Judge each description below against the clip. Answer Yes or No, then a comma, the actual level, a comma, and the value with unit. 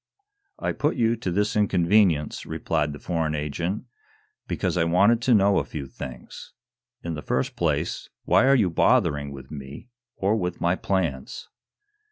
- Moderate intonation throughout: No, wide, 5.7 semitones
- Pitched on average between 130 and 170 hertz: No, very low, 85 Hz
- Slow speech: No, average, 160 wpm